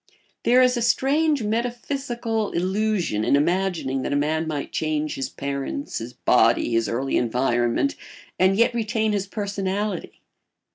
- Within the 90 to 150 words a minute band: Yes, average, 140 wpm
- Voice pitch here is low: No, high, 190 Hz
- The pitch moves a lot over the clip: Yes, wide, 8.9 semitones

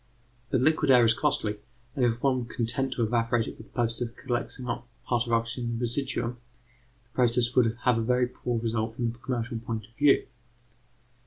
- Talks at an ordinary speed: No, fast, 215 wpm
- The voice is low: Yes, low, 120 Hz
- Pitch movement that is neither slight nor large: No, narrow, 1.5 semitones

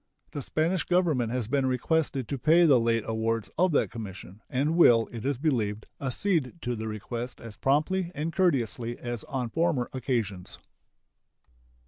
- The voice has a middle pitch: No, low, 125 Hz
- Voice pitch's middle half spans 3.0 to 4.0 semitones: No, wide, 5.4 semitones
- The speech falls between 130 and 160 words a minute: Yes, average, 155 wpm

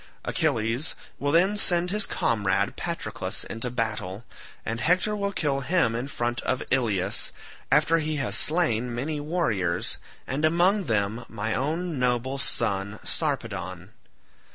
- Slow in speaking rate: Yes, slow, 130 wpm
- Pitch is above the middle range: No, low, 125 Hz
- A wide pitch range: Yes, wide, 6.3 semitones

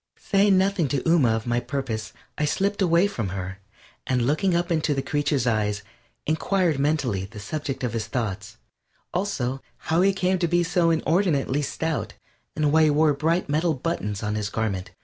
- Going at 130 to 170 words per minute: No, average, 180 wpm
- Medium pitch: Yes, medium, 145 Hz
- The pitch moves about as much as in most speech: No, wide, 6.7 semitones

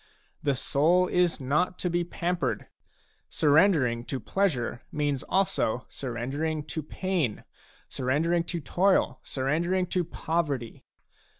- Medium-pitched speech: Yes, medium, 155 Hz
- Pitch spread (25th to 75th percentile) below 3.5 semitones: No, average, 5.0 semitones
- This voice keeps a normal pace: No, slow, 110 wpm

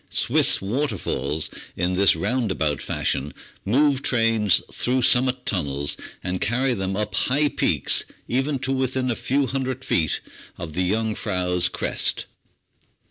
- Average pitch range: No, wide, 6.3 semitones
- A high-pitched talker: No, low, 115 Hz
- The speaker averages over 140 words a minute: No, slow, 135 wpm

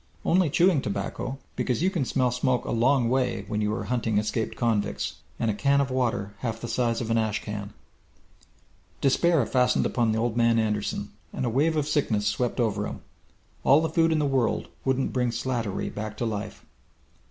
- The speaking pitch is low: Yes, low, 120 Hz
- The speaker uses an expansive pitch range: No, average, 3.7 semitones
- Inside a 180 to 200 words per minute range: Yes, average, 190 wpm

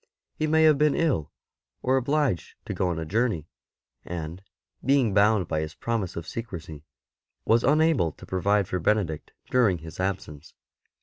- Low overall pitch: Yes, low, 100 Hz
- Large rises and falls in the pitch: Yes, wide, 7.5 semitones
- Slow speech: No, average, 160 wpm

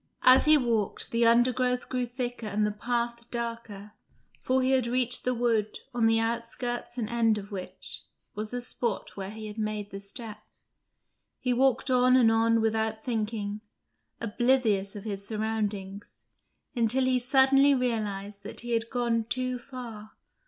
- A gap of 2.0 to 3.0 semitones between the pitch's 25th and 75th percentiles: Yes, average, 2.7 semitones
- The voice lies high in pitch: Yes, high, 230 Hz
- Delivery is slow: No, average, 160 wpm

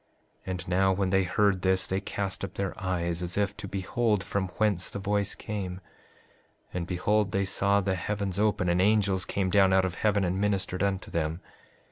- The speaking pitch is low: Yes, very low, 95 Hz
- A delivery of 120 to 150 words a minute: No, average, 195 wpm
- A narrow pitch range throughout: Yes, narrow, 1.6 semitones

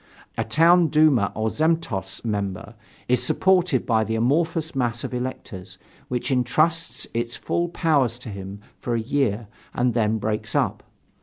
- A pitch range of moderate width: No, wide, 6.0 semitones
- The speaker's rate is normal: Yes, average, 150 wpm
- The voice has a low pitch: Yes, low, 120 Hz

